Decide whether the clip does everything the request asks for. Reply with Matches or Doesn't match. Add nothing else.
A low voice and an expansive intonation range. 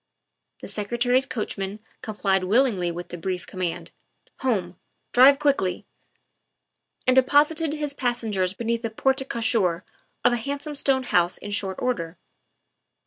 Doesn't match